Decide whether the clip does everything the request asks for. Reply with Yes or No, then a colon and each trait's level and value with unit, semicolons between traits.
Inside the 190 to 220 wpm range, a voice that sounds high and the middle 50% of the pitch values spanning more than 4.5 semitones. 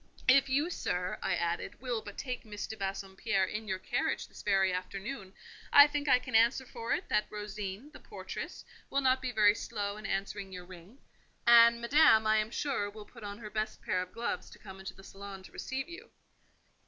No: fast, 205 wpm; high, 215 Hz; average, 4.1 semitones